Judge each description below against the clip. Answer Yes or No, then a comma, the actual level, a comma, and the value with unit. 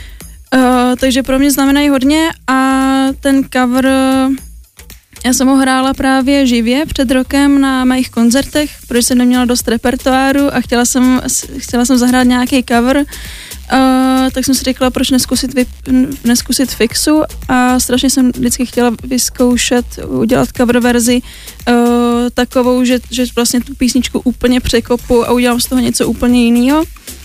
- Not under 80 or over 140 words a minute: No, average, 150 wpm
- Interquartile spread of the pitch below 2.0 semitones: Yes, narrow, 1.4 semitones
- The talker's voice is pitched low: No, very high, 255 Hz